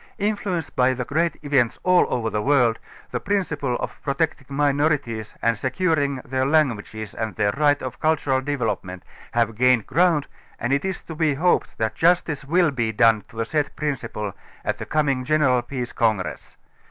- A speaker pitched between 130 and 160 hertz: Yes, low, 135 Hz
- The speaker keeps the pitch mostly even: No, average, 4.9 semitones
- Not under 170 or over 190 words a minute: Yes, average, 175 wpm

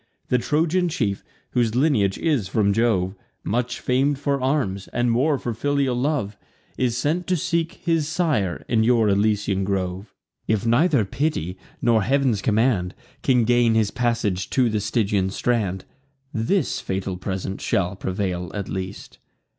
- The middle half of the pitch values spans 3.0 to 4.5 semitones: No, wide, 5.6 semitones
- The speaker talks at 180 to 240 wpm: No, average, 145 wpm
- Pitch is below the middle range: Yes, low, 115 Hz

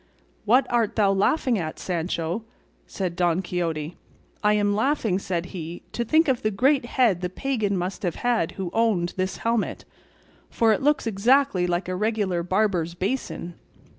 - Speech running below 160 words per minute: No, average, 165 wpm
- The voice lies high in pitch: Yes, high, 195 Hz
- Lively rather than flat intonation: No, average, 4.7 semitones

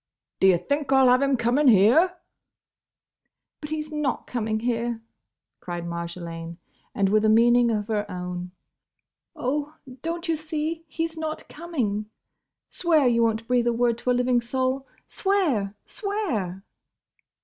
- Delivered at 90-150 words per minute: Yes, average, 140 wpm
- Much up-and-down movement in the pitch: Yes, wide, 6.2 semitones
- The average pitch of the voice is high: Yes, high, 245 Hz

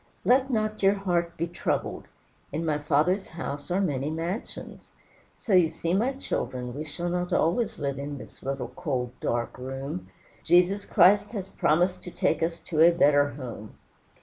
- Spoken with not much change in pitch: No, average, 4.6 semitones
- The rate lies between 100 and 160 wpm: No, average, 170 wpm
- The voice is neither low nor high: Yes, medium, 165 Hz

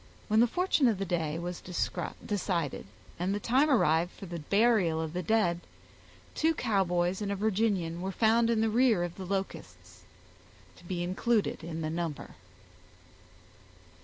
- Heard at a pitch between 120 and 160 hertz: No, high, 190 Hz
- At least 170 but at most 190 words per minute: No, average, 160 wpm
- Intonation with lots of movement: No, average, 4.4 semitones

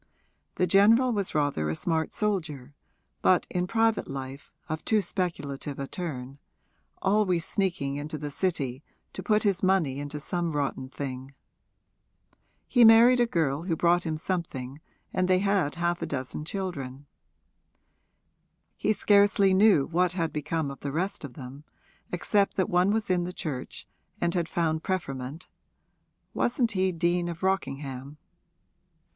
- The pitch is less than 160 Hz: No, medium, 170 Hz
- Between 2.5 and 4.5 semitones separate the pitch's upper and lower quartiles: No, average, 5.0 semitones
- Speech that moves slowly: No, average, 145 wpm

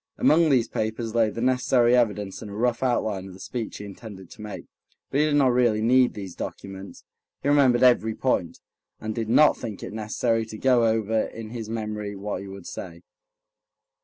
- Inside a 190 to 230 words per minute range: Yes, average, 195 wpm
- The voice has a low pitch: Yes, low, 110 Hz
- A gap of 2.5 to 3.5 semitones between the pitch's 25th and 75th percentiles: Yes, average, 3.0 semitones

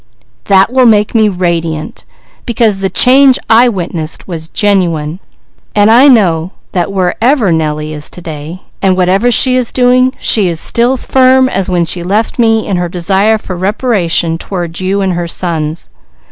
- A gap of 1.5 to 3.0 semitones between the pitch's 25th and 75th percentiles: No, average, 5.0 semitones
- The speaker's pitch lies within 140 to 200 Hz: Yes, high, 190 Hz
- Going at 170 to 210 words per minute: No, average, 160 wpm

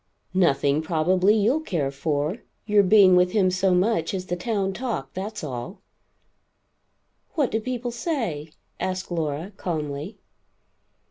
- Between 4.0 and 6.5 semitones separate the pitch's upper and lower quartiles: Yes, average, 5.2 semitones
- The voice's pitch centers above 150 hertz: Yes, medium, 185 Hz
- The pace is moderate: No, slow, 130 wpm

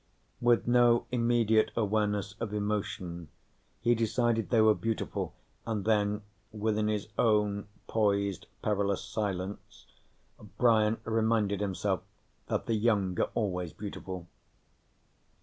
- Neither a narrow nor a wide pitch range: No, narrow, 2.0 semitones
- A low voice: Yes, low, 105 Hz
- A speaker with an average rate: No, slow, 110 wpm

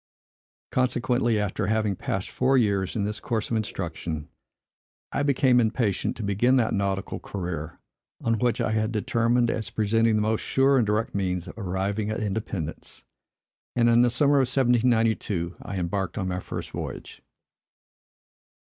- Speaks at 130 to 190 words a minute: Yes, average, 155 wpm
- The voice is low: Yes, low, 110 Hz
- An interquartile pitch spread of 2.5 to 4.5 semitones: Yes, average, 3.6 semitones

